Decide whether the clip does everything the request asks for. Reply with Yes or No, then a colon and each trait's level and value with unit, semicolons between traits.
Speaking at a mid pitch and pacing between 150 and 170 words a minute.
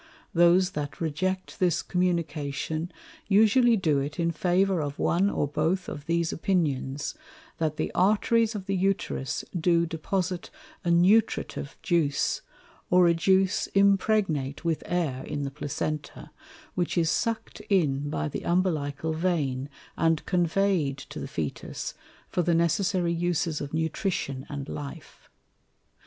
No: medium, 170 Hz; slow, 135 wpm